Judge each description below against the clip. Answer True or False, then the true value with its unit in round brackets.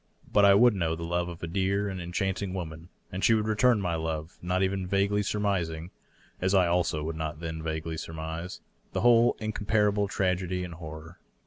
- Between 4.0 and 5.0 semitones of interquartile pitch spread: False (3.4 semitones)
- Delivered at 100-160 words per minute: False (190 wpm)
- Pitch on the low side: True (90 Hz)